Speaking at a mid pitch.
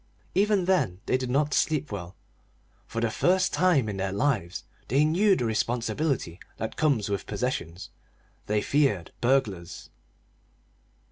No: low, 125 Hz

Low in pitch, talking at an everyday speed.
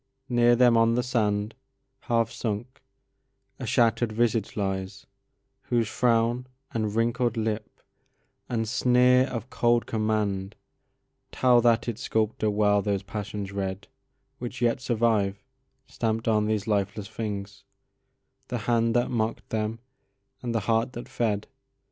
No: low, 115 Hz; slow, 115 wpm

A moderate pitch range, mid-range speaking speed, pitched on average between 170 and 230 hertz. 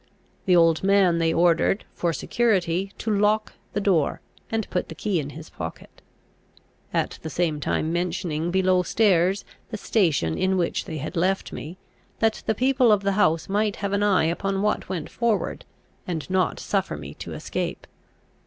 Yes: average, 3.6 semitones; average, 170 wpm; medium, 185 Hz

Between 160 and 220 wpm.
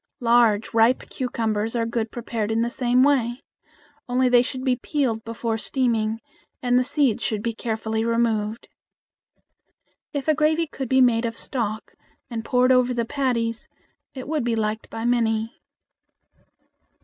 No: average, 150 wpm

